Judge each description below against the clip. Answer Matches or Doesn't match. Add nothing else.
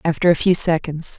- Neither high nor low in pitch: Matches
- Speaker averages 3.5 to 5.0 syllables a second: Doesn't match